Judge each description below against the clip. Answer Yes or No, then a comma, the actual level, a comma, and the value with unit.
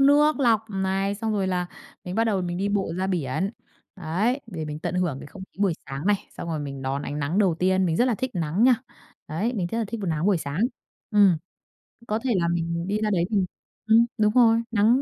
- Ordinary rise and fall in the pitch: Yes, average, 4.5 semitones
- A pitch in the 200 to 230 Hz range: No, high, 190 Hz